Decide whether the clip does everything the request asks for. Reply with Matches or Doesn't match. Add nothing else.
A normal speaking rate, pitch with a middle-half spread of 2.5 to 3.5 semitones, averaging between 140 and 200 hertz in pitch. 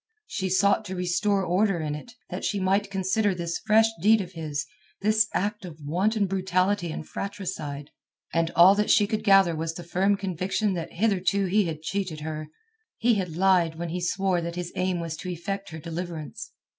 Matches